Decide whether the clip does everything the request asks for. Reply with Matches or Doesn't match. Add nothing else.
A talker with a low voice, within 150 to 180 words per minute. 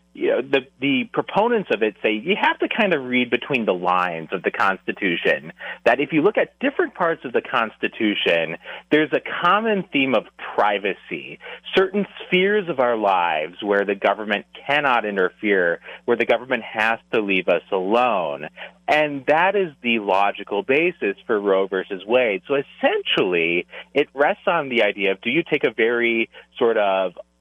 Matches